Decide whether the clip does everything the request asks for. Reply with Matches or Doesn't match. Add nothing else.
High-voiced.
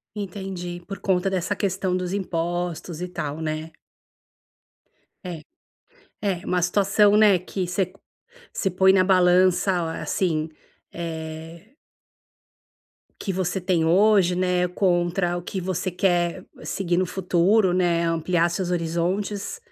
Doesn't match